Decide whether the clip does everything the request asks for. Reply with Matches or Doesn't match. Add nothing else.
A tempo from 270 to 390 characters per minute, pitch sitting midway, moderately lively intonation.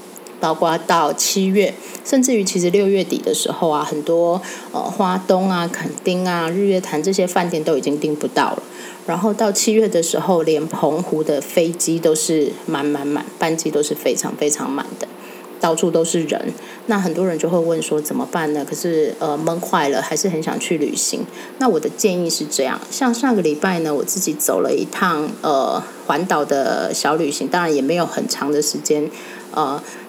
Matches